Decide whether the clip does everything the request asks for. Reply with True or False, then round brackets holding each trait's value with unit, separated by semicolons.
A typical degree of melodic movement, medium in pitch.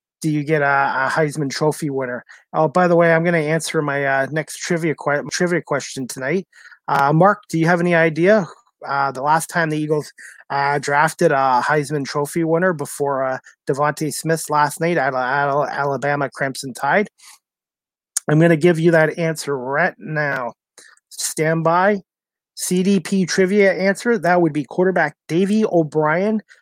True (3.4 semitones; 155 Hz)